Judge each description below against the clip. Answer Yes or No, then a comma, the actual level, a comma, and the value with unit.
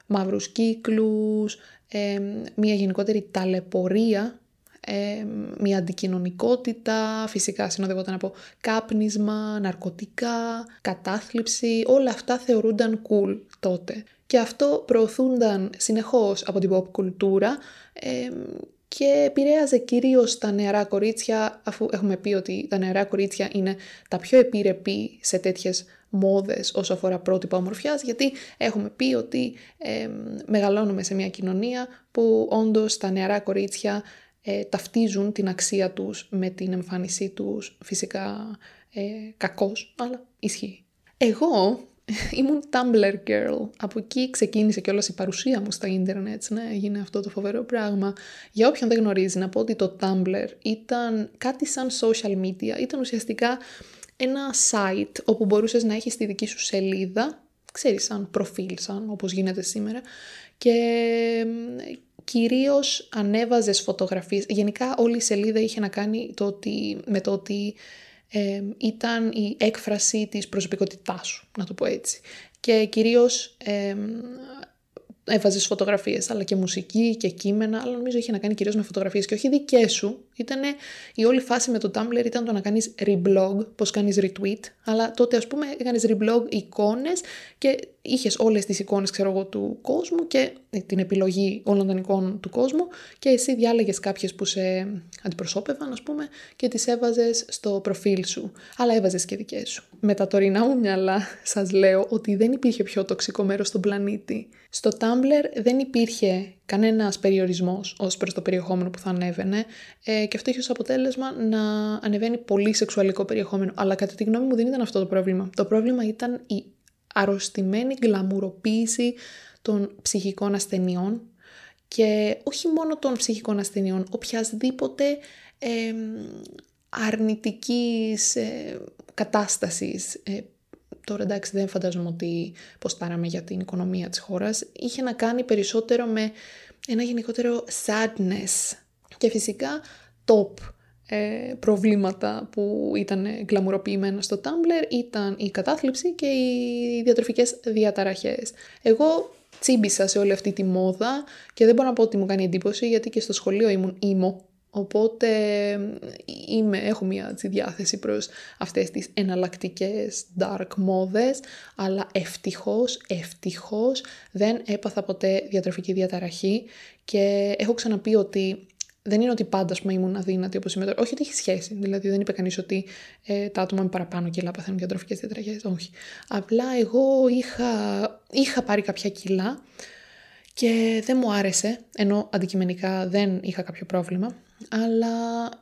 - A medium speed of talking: Yes, average, 140 wpm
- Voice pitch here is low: No, high, 210 Hz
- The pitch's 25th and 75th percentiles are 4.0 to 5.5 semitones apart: No, average, 3.2 semitones